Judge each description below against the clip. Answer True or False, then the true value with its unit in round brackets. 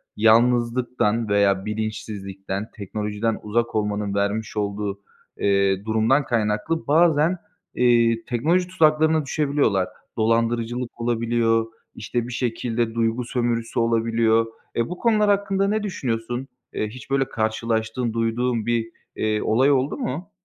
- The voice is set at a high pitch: False (115 Hz)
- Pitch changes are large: False (2.8 semitones)